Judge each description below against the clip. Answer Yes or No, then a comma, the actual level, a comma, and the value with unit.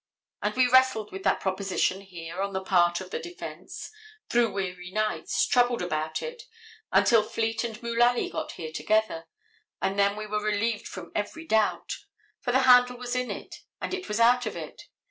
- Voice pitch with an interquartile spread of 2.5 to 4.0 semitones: No, average, 4.4 semitones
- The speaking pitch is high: Yes, high, 215 Hz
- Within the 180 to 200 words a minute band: Yes, average, 185 wpm